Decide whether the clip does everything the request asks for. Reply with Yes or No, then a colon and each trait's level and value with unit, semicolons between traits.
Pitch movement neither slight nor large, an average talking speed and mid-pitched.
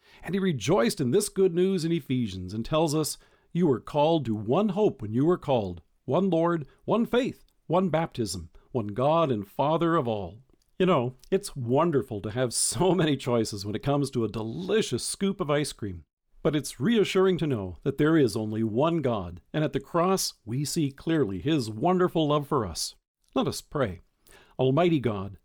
No: wide, 7.3 semitones; average, 190 wpm; medium, 145 Hz